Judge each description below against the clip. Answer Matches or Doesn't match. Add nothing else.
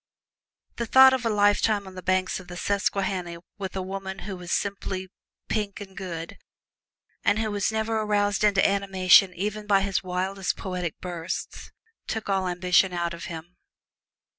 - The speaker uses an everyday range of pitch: Doesn't match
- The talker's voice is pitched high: Matches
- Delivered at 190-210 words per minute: Doesn't match